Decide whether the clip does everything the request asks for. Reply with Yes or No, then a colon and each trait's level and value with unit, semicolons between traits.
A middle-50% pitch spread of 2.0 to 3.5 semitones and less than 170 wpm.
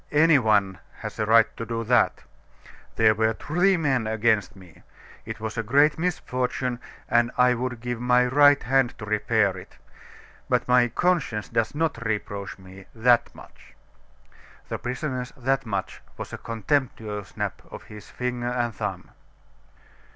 Yes: average, 2.8 semitones; average, 150 wpm